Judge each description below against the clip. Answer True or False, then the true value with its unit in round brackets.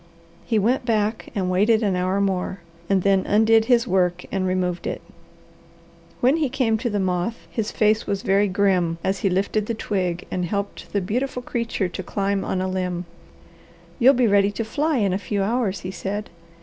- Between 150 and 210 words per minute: True (190 wpm)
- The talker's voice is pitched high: True (200 Hz)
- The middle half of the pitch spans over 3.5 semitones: False (3.2 semitones)